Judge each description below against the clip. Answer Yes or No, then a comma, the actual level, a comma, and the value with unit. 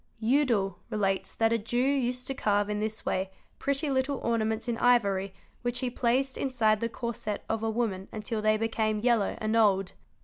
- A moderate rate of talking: Yes, average, 180 wpm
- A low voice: No, high, 225 Hz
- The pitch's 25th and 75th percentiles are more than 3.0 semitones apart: No, average, 2.7 semitones